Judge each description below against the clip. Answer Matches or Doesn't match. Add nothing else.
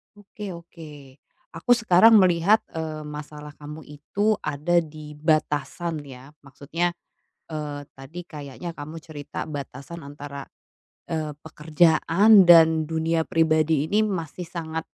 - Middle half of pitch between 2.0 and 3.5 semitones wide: Matches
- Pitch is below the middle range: Doesn't match